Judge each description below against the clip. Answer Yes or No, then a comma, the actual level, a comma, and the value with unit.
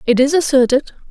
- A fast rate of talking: No, average, 165 wpm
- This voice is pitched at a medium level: No, very high, 270 Hz